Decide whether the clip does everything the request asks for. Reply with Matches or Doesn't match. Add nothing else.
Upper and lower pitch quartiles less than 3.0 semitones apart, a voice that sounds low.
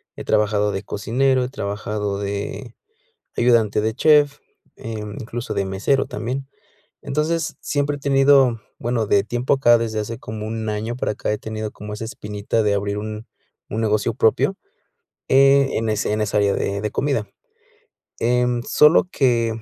Doesn't match